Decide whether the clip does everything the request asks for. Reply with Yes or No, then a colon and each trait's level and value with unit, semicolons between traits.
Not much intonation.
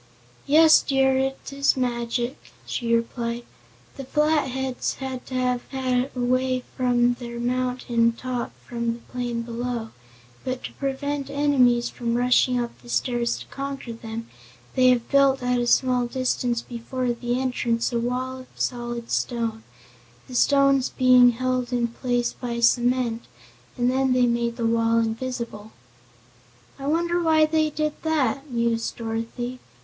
Yes: narrow, 1.8 semitones